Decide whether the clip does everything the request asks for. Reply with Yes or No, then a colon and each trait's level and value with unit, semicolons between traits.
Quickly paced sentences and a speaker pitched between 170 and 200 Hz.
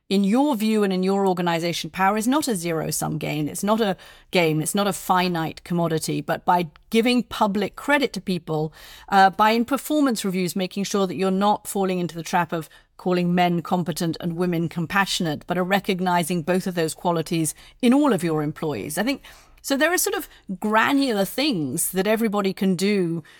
No: average, 195 wpm; high, 190 Hz